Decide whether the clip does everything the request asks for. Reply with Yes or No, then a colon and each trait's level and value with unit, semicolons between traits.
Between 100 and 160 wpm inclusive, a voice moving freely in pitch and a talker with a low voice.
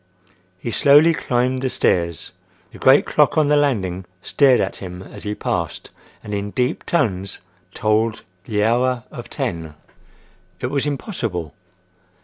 Yes: slow, 135 wpm; wide, 6.1 semitones; low, 115 Hz